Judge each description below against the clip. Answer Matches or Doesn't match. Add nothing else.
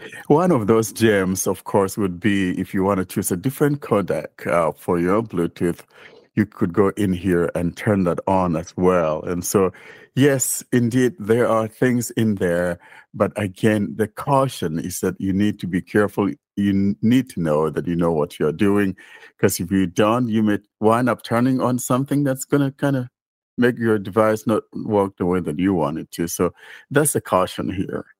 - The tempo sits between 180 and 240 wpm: Matches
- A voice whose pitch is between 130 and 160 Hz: Doesn't match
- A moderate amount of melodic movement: Matches